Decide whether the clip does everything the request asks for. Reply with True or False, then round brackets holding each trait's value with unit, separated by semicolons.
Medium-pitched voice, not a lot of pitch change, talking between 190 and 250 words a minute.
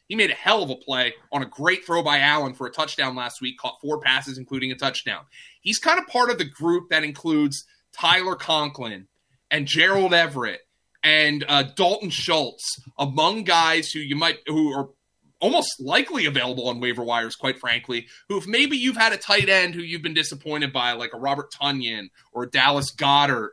False (145 Hz; 4.3 semitones; 200 wpm)